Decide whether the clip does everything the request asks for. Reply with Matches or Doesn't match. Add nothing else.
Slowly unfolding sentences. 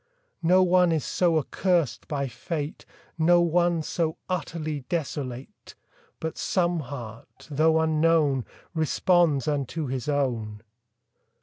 Matches